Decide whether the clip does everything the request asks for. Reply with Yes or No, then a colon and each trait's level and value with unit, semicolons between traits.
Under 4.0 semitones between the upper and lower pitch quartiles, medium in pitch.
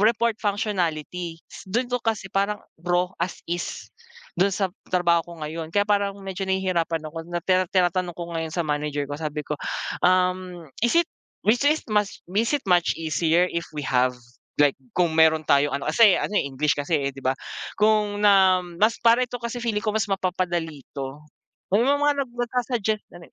No: average, 4.5 semitones; medium, 180 Hz